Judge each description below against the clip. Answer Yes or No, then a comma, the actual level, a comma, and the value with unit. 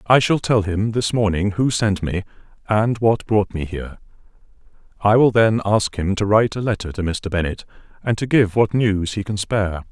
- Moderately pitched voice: No, low, 105 Hz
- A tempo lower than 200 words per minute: No, fast, 205 wpm